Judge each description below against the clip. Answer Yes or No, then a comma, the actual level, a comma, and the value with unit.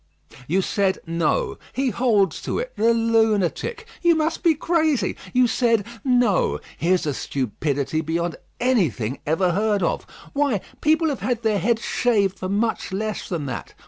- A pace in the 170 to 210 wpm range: No, average, 155 wpm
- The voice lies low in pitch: No, high, 215 Hz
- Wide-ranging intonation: Yes, wide, 6.3 semitones